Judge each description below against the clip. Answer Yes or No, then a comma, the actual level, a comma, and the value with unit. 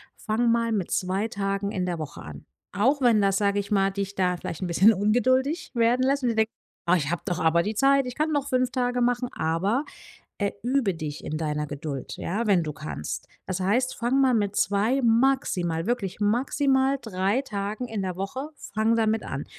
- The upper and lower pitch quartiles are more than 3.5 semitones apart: Yes, average, 5.2 semitones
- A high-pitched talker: Yes, high, 210 Hz